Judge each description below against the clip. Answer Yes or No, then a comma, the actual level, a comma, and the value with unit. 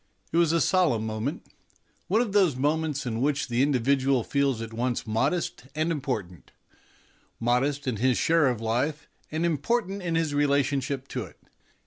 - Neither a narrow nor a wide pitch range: Yes, average, 4.6 semitones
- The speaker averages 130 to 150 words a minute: No, average, 165 wpm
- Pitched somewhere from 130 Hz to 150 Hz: Yes, medium, 140 Hz